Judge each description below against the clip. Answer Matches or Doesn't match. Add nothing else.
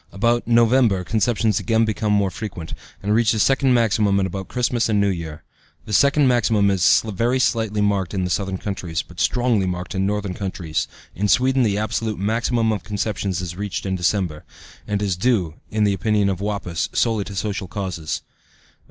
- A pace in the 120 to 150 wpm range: Doesn't match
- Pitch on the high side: Doesn't match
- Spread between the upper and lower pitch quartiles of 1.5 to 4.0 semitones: Matches